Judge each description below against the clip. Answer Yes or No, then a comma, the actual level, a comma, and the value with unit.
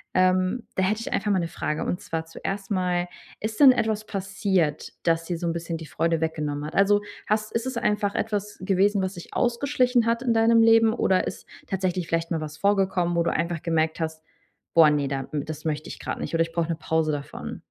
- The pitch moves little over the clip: No, average, 4.2 semitones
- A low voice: No, medium, 185 Hz